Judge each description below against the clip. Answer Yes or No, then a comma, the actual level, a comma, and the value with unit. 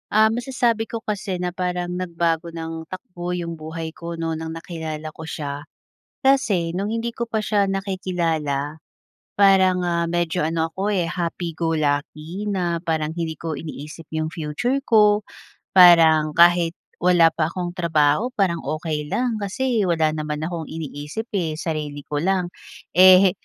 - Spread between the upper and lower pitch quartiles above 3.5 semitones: No, average, 3.0 semitones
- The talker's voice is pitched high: No, medium, 170 Hz